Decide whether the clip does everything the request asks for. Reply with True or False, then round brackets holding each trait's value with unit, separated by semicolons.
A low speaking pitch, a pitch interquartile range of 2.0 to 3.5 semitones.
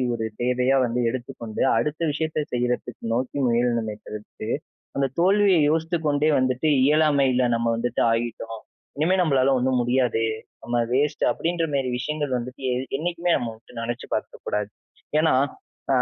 False (130 Hz; 4.2 semitones)